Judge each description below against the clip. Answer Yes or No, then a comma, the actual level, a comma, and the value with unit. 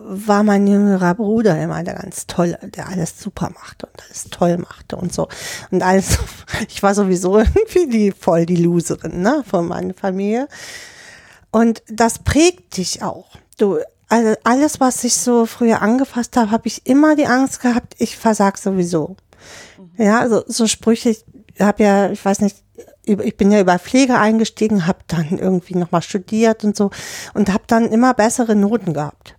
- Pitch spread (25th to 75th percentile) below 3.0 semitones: No, average, 3.8 semitones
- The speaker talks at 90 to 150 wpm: No, average, 175 wpm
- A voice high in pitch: Yes, high, 210 Hz